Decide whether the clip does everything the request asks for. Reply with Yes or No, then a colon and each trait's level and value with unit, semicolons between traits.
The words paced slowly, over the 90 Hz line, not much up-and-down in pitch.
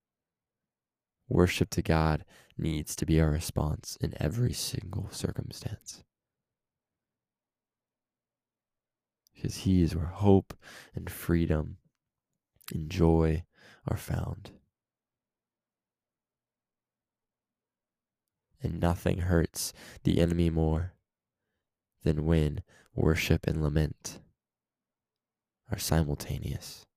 No: slow, 80 wpm; very low, 85 Hz; narrow, 2.3 semitones